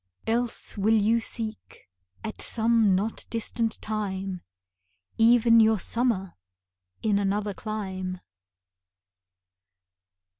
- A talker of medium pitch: No, high, 215 Hz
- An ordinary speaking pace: No, slow, 85 wpm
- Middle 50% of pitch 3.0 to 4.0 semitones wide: No, narrow, 2.5 semitones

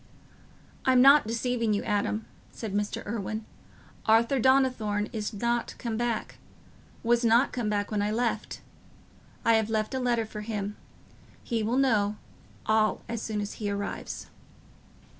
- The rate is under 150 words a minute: Yes, average, 140 wpm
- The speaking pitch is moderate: No, high, 220 Hz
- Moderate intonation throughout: No, narrow, 2.2 semitones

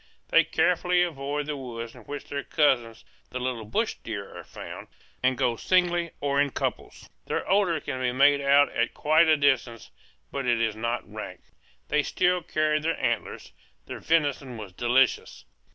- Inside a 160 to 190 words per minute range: Yes, average, 170 wpm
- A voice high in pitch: No, medium, 140 Hz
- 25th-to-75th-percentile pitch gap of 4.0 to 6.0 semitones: Yes, average, 4.3 semitones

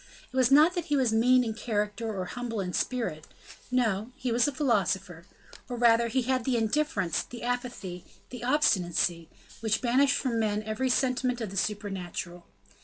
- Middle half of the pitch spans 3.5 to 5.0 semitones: Yes, average, 3.8 semitones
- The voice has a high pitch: Yes, high, 230 Hz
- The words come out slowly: No, average, 175 wpm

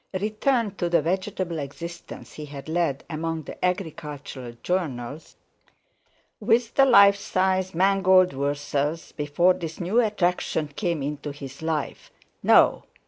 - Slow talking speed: Yes, slow, 120 wpm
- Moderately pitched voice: Yes, medium, 170 Hz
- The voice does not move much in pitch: No, average, 4.3 semitones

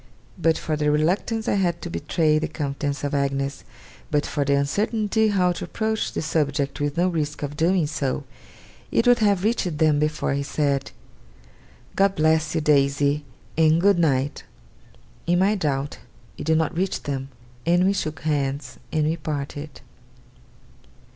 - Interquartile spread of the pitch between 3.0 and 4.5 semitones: Yes, average, 3.7 semitones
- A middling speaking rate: Yes, average, 160 wpm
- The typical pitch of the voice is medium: Yes, medium, 155 Hz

